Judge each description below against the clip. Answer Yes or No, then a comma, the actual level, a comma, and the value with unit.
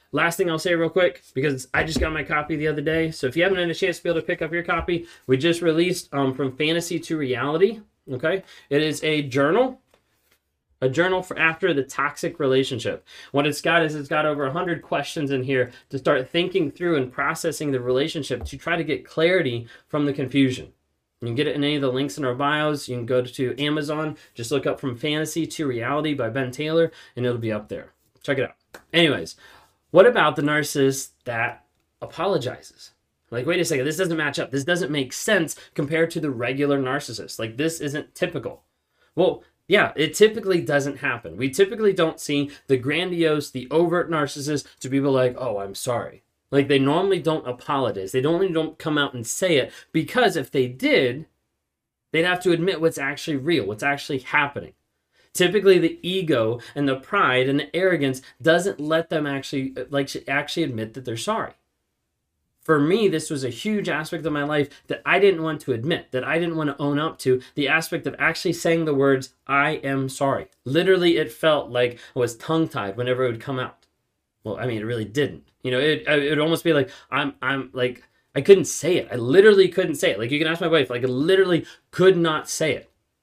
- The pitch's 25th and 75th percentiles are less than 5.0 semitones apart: Yes, average, 4.0 semitones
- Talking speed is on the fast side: Yes, fast, 210 wpm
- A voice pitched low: No, medium, 145 Hz